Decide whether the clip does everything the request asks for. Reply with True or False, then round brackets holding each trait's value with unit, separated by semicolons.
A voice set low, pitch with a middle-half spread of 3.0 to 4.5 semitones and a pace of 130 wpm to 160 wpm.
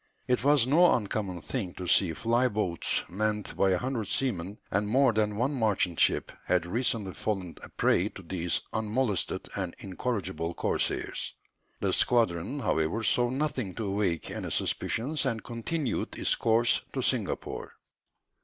False (110 Hz; 4.9 semitones; 150 wpm)